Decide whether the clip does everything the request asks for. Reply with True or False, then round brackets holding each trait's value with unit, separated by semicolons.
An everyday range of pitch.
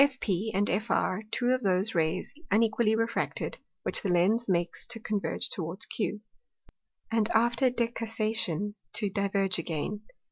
True (3.3 semitones)